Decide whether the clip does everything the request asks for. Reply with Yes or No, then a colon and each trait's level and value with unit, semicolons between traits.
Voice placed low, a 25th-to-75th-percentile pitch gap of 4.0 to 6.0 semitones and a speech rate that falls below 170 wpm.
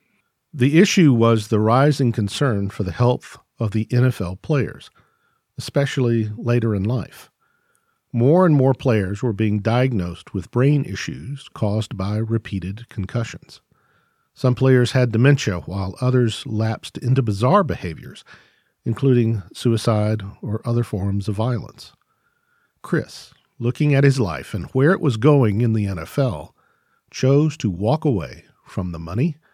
Yes: low, 120 Hz; average, 4.4 semitones; average, 140 wpm